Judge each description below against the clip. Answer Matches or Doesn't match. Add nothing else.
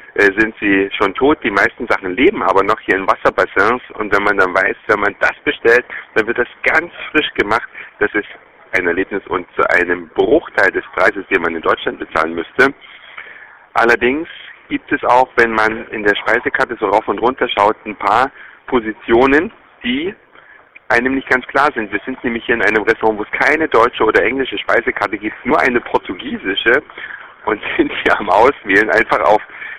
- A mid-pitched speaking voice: Doesn't match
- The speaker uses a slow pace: Doesn't match